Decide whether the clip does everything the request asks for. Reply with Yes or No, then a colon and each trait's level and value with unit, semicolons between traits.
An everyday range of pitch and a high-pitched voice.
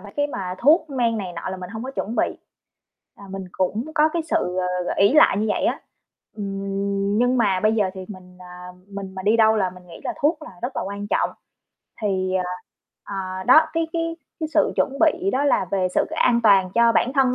No: wide, 5.8 semitones; high, 210 Hz